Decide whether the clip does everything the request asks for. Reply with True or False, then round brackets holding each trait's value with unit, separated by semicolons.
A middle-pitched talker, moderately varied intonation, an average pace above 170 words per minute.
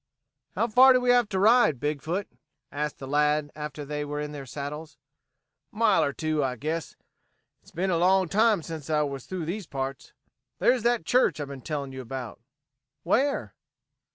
False (155 Hz; 5.7 semitones; 180 wpm)